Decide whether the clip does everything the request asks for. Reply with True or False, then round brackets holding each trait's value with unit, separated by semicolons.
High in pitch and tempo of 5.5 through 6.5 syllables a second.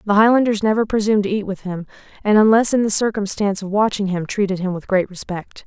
True (205 Hz; 6.4 syllables/s)